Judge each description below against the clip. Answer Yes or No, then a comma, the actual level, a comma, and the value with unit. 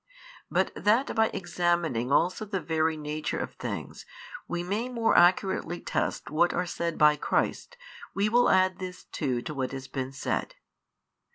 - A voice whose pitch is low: No, medium, 175 Hz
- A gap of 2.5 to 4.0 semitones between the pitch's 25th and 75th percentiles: No, average, 4.4 semitones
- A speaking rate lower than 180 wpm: Yes, average, 160 wpm